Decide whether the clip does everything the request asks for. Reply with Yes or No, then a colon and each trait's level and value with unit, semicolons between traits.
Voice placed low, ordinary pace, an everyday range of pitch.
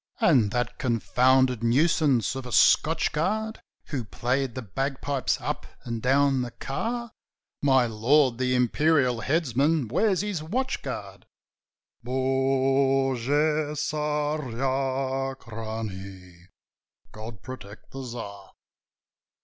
No: low, 130 Hz; slow, 100 wpm; average, 3.8 semitones